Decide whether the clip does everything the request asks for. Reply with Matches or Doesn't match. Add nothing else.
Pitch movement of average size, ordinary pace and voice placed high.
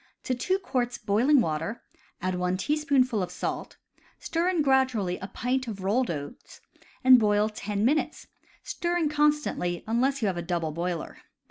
Doesn't match